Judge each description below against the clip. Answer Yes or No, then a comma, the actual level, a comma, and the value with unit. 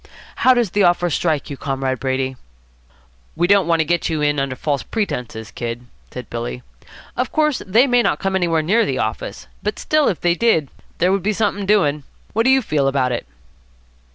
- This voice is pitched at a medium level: Yes, medium, 170 Hz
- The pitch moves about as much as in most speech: No, wide, 7.4 semitones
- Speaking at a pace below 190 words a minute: No, average, 200 wpm